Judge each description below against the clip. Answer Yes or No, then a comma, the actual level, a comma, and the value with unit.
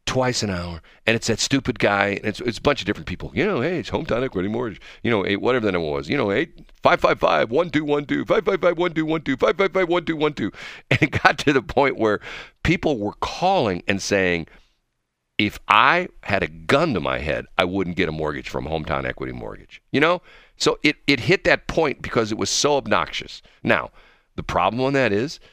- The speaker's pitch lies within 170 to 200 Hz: No, low, 110 Hz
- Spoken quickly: Yes, fast, 245 wpm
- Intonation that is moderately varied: No, wide, 7.7 semitones